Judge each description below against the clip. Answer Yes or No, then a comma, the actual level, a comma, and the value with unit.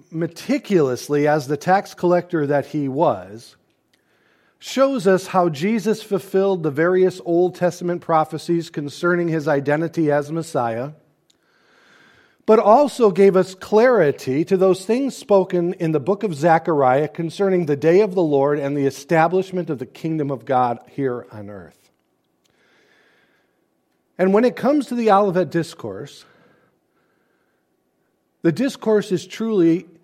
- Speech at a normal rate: No, slow, 130 wpm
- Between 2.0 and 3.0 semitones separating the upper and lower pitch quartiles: No, average, 4.4 semitones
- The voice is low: No, medium, 170 Hz